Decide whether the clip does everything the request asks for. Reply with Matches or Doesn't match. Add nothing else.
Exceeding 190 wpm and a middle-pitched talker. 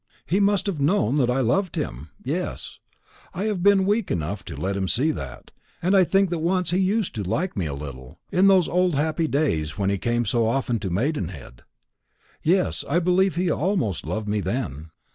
Matches